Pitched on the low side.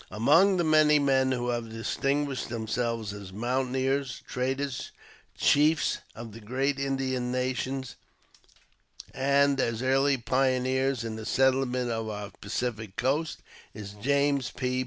Yes: low, 130 Hz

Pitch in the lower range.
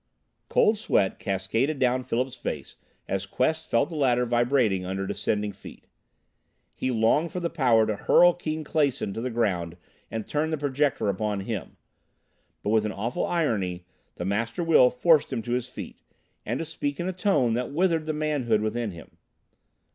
Yes: low, 125 Hz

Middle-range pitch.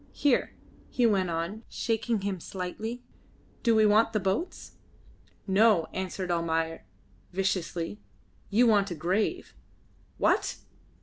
No: high, 195 Hz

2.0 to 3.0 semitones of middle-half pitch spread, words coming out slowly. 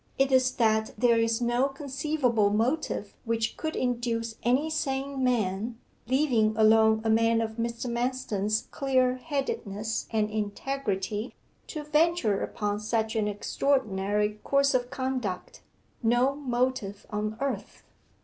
No: average, 3.6 semitones; slow, 125 wpm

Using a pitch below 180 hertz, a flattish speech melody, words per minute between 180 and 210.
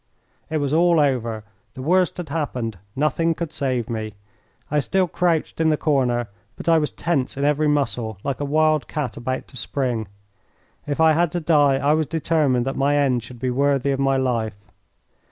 No: medium, 140 Hz; average, 3.6 semitones; average, 190 wpm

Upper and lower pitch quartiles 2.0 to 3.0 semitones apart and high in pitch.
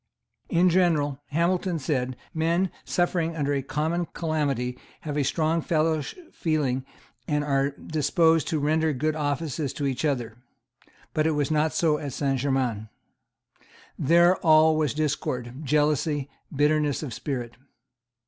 No: narrow, 2.6 semitones; medium, 150 Hz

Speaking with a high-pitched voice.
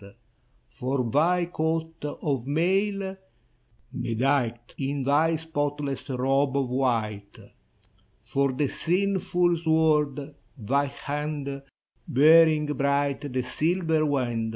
No: medium, 145 Hz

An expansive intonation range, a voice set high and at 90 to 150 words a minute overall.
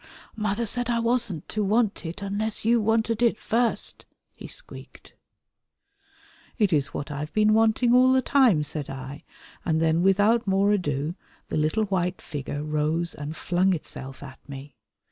No: wide, 6.7 semitones; high, 195 Hz; average, 165 wpm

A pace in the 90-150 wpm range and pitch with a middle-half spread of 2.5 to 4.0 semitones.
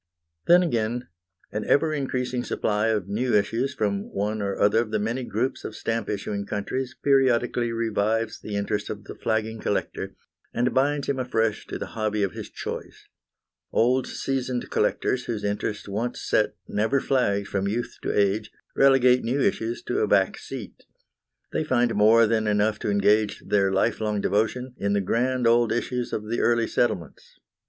No: average, 170 wpm; average, 3.1 semitones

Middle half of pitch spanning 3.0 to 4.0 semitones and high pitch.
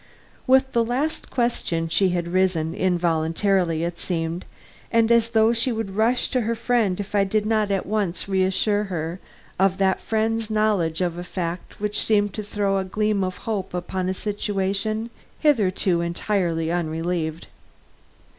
Yes: average, 3.7 semitones; high, 195 Hz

